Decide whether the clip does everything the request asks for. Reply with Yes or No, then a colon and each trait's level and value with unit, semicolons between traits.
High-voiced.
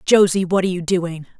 No: medium, 180 Hz